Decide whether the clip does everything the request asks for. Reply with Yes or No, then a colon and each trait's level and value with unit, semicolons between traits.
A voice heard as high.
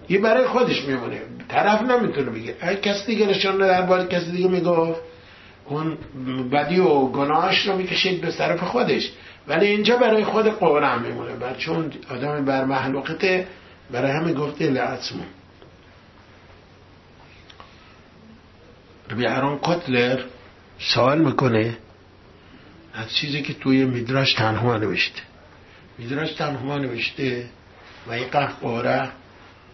No: low, 135 Hz